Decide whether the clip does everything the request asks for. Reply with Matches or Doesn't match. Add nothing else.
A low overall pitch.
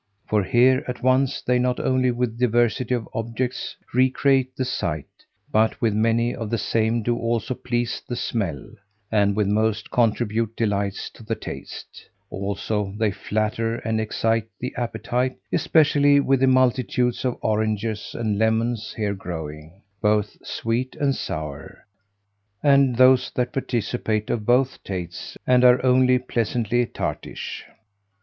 Matches